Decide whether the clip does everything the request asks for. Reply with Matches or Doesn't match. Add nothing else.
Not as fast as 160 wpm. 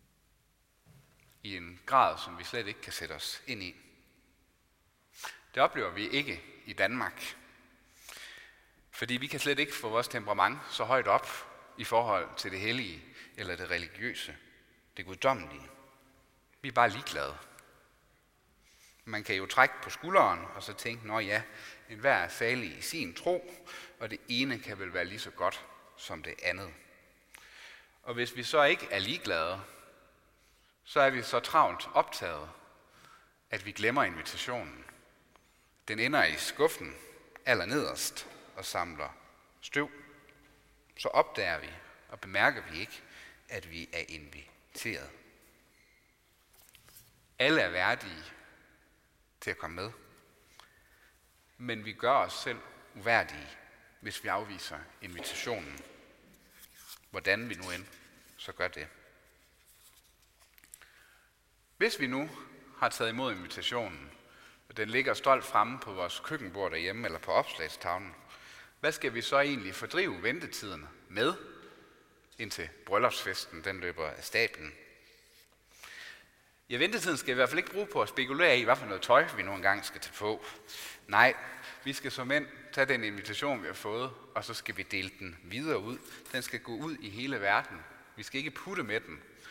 Matches